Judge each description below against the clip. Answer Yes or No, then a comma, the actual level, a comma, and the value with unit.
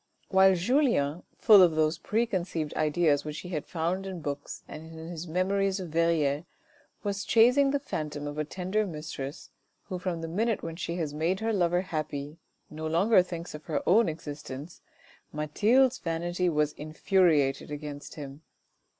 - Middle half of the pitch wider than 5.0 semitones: No, average, 3.9 semitones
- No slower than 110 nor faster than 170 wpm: Yes, average, 160 wpm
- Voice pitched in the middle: Yes, medium, 170 Hz